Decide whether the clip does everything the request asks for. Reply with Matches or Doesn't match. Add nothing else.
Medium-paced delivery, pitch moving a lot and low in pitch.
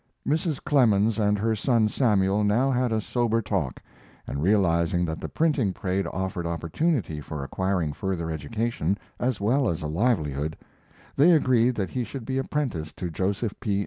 Matches